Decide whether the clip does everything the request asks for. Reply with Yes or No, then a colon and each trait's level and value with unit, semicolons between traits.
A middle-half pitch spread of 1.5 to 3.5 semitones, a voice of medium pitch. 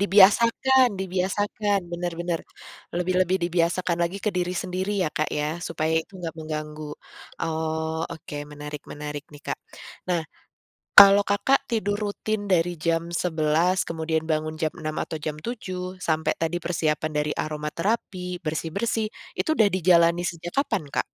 Yes: average, 3.2 semitones; medium, 170 Hz